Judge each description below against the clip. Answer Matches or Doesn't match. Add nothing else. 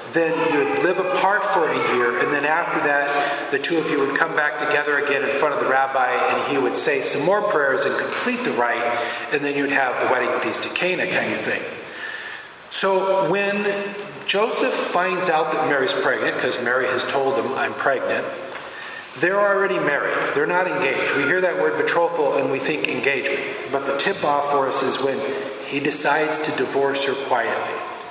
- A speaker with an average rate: Matches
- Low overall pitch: Doesn't match